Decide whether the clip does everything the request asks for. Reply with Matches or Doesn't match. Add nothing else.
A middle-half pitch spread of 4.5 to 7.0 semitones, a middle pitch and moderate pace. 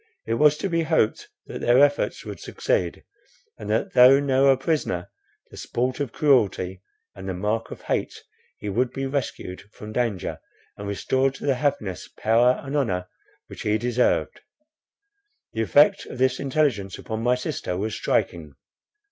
Doesn't match